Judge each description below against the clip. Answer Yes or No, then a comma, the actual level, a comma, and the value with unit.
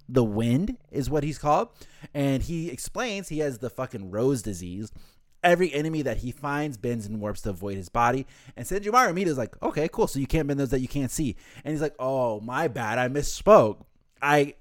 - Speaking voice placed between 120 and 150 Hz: Yes, low, 135 Hz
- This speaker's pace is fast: Yes, fast, 210 wpm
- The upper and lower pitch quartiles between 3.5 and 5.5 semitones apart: Yes, average, 4.3 semitones